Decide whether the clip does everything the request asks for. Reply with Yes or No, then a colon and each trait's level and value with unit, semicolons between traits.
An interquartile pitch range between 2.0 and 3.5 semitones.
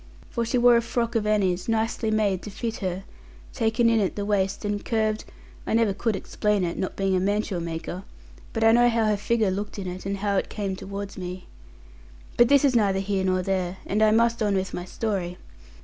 Yes: average, 2.8 semitones